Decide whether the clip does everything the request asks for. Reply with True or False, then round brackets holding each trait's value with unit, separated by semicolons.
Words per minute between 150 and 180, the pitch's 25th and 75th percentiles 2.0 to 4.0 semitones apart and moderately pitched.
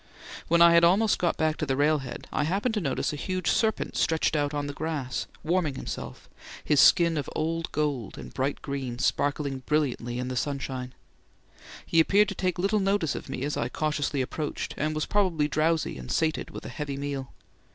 False (195 wpm; 3.4 semitones; 150 Hz)